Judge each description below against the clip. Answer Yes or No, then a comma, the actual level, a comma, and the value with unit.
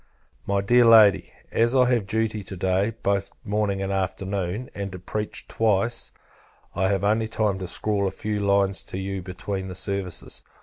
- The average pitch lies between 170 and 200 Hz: No, low, 100 Hz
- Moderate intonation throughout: No, narrow, 2.1 semitones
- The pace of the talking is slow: No, average, 175 wpm